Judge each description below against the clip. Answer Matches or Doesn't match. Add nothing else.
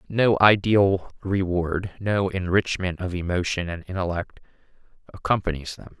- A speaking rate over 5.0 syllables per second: Doesn't match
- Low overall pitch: Matches